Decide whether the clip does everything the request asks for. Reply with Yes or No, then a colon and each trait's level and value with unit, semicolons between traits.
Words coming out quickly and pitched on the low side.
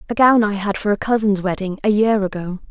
No: fast, 245 wpm; high, 205 Hz